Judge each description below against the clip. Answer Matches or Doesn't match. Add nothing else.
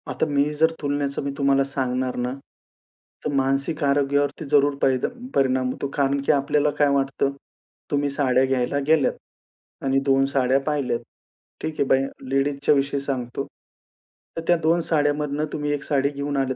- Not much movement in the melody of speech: Matches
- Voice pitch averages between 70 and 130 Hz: Doesn't match